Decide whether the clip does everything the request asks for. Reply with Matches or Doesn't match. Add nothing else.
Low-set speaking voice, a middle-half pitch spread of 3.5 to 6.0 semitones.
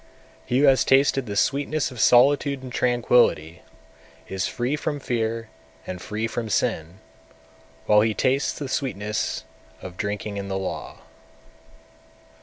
Matches